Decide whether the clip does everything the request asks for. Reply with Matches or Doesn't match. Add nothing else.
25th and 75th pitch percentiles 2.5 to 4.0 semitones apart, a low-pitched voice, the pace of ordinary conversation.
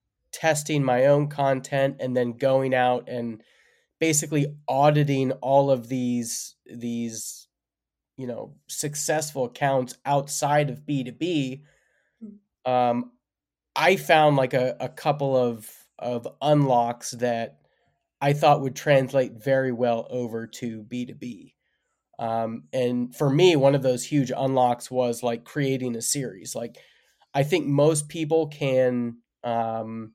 Doesn't match